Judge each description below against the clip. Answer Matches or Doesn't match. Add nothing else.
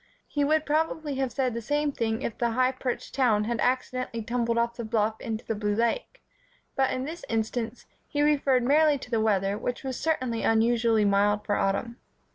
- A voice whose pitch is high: Matches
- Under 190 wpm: Doesn't match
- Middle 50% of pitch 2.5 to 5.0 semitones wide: Matches